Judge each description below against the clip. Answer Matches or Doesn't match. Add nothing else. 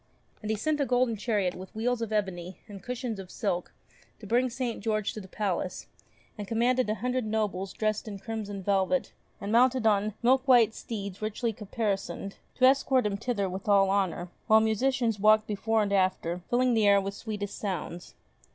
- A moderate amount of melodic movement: Matches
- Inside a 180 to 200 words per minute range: Matches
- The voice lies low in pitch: Doesn't match